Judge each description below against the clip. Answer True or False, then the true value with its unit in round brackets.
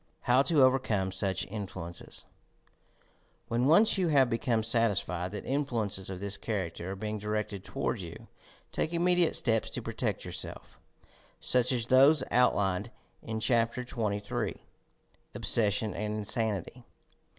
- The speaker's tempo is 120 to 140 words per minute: True (135 wpm)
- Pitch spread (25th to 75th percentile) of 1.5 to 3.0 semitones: False (4.0 semitones)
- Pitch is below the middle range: True (110 Hz)